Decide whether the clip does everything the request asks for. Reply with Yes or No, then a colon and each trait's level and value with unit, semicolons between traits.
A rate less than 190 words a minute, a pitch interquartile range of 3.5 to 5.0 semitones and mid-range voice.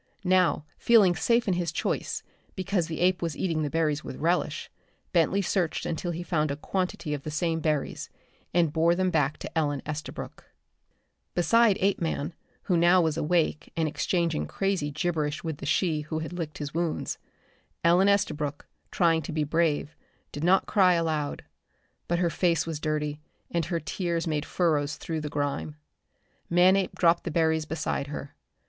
No: average, 165 wpm; average, 2.7 semitones; medium, 165 Hz